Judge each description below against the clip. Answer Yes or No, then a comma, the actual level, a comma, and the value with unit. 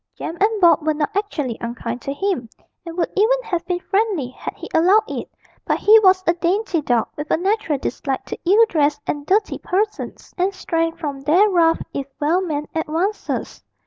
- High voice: Yes, very high, 340 Hz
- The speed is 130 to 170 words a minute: No, average, 190 wpm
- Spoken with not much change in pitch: No, average, 5.1 semitones